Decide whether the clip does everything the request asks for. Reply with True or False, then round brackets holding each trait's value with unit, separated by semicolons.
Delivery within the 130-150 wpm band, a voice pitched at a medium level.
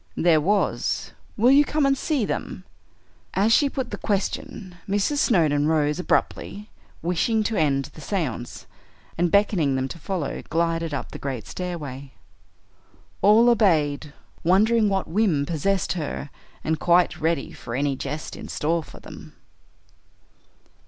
True (140 wpm; 170 Hz)